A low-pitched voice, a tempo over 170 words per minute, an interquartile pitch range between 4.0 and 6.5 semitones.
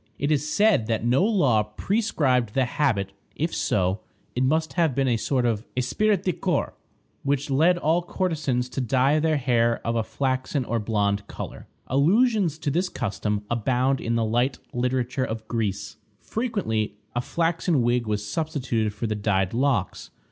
No: low, 130 Hz; average, 165 wpm; wide, 5.6 semitones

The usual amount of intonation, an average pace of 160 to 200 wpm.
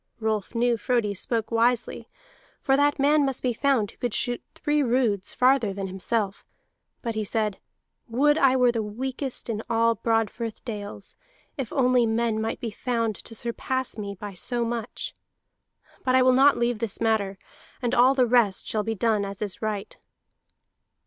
Yes: average, 3.0 semitones; average, 170 wpm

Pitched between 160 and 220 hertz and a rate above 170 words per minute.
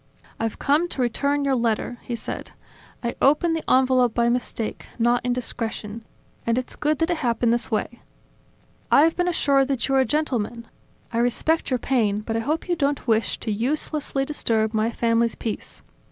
No: high, 245 Hz; average, 180 wpm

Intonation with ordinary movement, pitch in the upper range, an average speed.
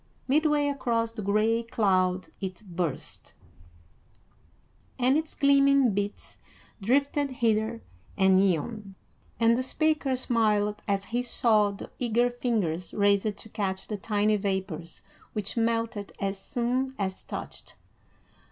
No: average, 3.8 semitones; high, 215 Hz; slow, 120 wpm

